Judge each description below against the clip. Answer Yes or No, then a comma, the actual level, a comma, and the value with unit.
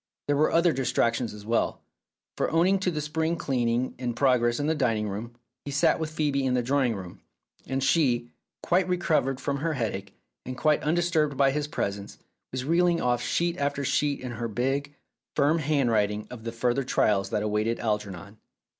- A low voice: Yes, low, 130 Hz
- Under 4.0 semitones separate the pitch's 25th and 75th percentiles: No, average, 4.5 semitones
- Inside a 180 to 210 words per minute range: Yes, average, 185 wpm